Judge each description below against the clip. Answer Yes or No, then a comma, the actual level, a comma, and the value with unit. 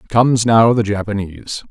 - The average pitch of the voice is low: Yes, low, 110 Hz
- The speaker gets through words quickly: No, average, 140 wpm